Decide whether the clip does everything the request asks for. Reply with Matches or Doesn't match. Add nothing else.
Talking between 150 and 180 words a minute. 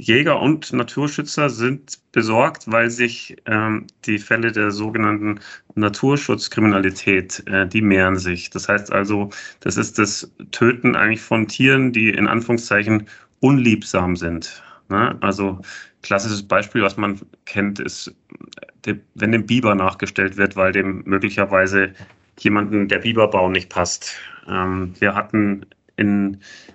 Doesn't match